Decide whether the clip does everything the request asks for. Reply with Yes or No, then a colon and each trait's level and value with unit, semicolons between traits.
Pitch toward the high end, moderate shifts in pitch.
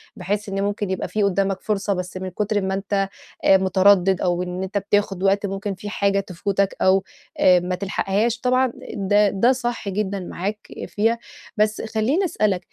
No: high, 200 Hz; narrow, 1.8 semitones